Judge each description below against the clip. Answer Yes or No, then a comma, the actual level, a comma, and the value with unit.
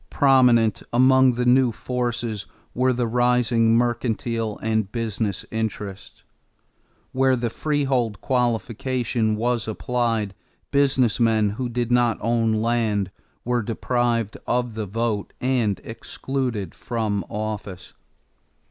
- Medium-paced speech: No, slow, 110 wpm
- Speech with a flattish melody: Yes, narrow, 2.1 semitones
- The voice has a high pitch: No, low, 115 Hz